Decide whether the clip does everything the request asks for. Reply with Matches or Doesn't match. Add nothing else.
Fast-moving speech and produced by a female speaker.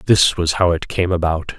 Doesn't match